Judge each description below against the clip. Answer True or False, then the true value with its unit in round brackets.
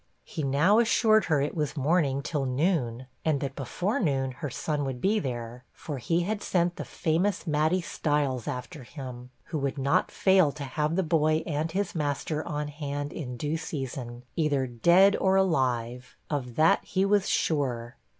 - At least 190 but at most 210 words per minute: False (175 wpm)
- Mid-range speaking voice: True (150 Hz)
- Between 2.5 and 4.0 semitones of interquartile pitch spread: False (4.4 semitones)